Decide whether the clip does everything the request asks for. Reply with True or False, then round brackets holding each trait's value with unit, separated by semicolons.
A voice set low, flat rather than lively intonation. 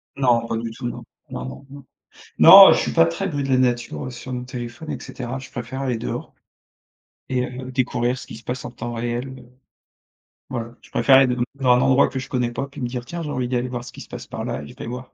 True (125 Hz; 1.7 semitones)